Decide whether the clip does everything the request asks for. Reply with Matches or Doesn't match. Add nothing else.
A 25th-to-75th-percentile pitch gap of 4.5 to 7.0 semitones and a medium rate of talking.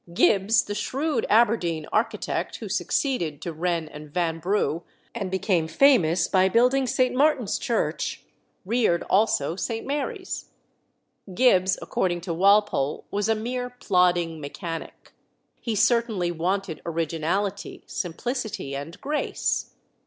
Doesn't match